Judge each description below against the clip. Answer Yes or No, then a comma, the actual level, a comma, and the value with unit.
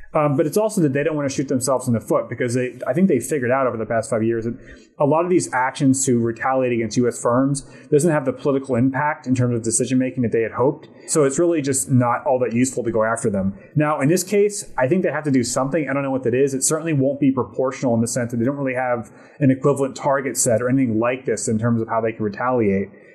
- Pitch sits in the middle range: No, low, 130 Hz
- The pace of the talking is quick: Yes, fast, 280 wpm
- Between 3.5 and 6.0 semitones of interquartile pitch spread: No, average, 3.0 semitones